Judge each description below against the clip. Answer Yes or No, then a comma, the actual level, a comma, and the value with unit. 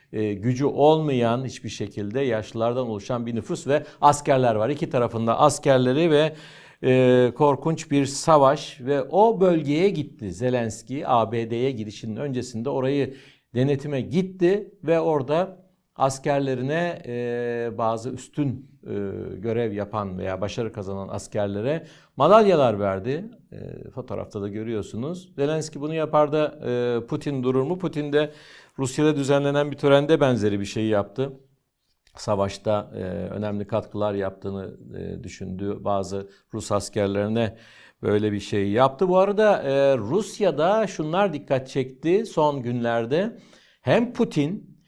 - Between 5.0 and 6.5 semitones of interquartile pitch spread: Yes, wide, 5.5 semitones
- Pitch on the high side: No, low, 130 Hz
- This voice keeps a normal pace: Yes, average, 120 wpm